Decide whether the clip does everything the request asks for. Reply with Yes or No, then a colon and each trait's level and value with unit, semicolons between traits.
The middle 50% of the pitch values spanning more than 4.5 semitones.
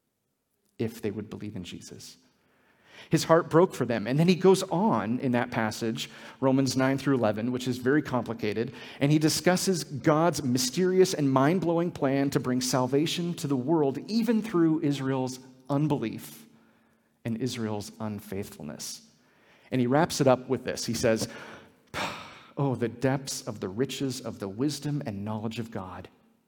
Yes: average, 4.9 semitones